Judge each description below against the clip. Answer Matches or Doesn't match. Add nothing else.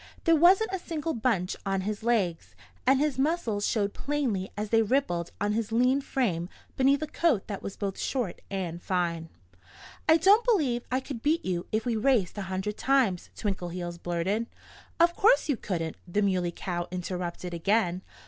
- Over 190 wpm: Doesn't match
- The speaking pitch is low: Doesn't match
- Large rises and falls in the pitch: Matches